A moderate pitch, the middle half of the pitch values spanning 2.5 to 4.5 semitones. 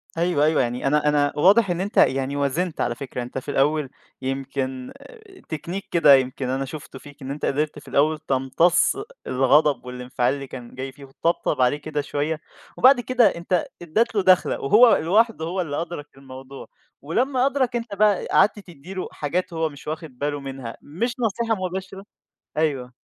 No: medium, 150 Hz; average, 5.2 semitones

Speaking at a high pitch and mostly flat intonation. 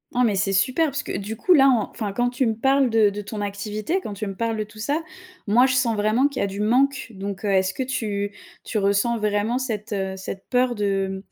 No: high, 215 Hz; average, 4.0 semitones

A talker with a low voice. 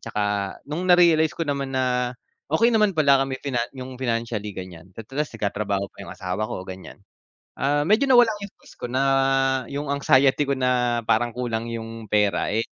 Yes: low, 125 Hz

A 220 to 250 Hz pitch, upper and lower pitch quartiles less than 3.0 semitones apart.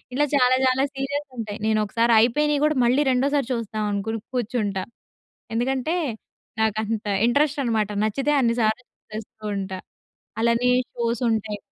No: high, 235 Hz; average, 3.7 semitones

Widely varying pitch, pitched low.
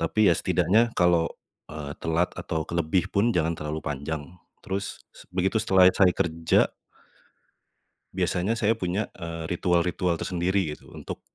No: average, 2.9 semitones; very low, 90 Hz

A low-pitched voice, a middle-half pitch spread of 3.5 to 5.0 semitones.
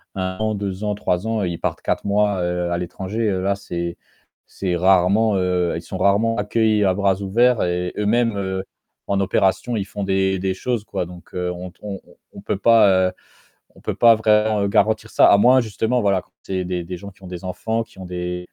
No: very low, 95 Hz; average, 2.8 semitones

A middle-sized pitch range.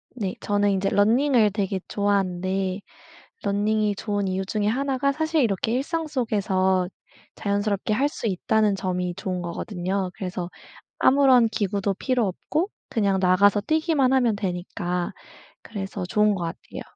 Yes: average, 3.8 semitones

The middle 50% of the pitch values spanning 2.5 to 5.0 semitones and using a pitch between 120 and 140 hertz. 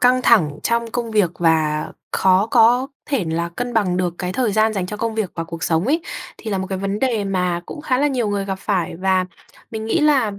No: average, 4.4 semitones; high, 205 Hz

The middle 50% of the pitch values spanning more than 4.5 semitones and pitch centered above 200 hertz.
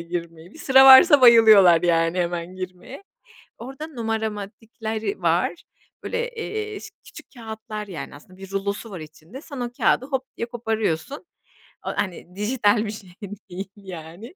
Yes: wide, 5.4 semitones; high, 210 Hz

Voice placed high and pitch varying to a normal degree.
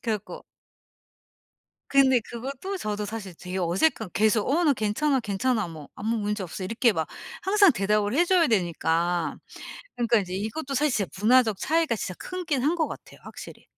No: high, 225 Hz; wide, 5.9 semitones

